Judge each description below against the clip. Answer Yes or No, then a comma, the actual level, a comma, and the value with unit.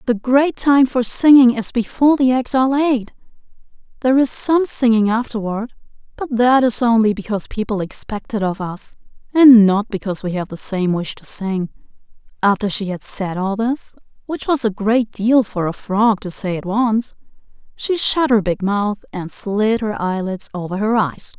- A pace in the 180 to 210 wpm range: Yes, average, 185 wpm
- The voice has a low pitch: No, high, 220 Hz